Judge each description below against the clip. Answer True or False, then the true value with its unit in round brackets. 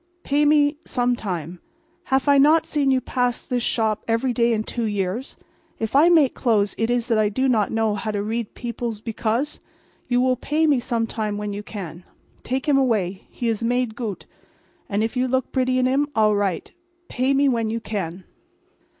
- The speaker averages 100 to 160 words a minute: False (200 wpm)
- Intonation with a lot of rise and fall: False (3.5 semitones)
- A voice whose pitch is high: True (235 Hz)